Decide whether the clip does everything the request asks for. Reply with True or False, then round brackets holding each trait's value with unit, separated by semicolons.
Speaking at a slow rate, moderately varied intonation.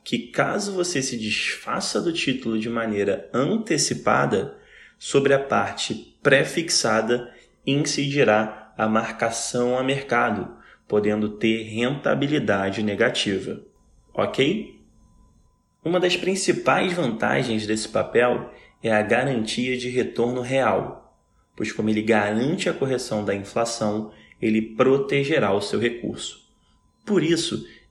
True (110 wpm; 3.8 semitones)